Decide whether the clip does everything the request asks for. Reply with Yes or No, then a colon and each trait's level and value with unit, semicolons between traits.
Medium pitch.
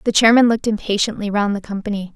No: high, 210 Hz